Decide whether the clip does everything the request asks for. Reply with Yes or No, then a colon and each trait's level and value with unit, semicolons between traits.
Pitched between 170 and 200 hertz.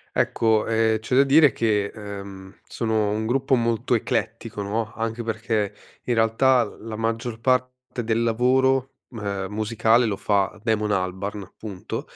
No: low, 110 Hz